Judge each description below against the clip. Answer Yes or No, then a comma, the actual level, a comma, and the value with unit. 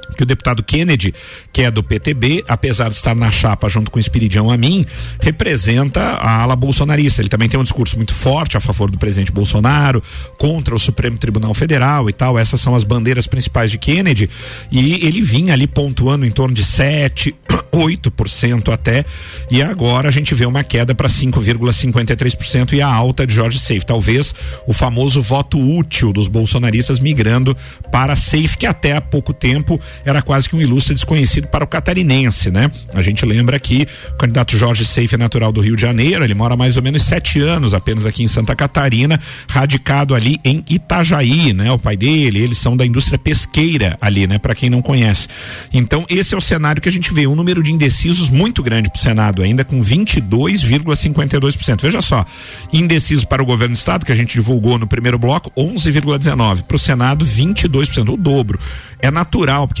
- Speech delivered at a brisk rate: Yes, fast, 195 wpm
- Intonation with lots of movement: No, average, 4.0 semitones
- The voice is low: Yes, low, 125 Hz